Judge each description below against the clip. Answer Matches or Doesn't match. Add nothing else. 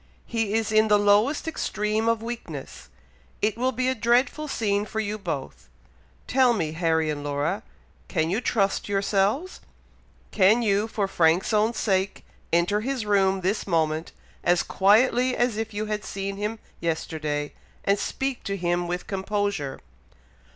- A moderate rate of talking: Matches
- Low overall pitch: Doesn't match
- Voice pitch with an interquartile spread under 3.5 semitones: Doesn't match